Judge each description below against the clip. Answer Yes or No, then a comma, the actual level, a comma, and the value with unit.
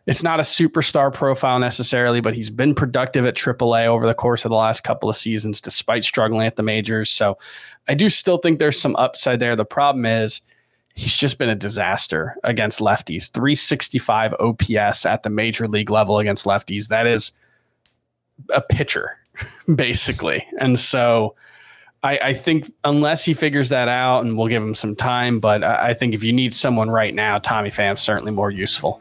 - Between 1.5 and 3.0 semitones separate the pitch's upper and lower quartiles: No, average, 3.7 semitones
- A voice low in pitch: Yes, low, 115 Hz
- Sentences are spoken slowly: No, average, 185 wpm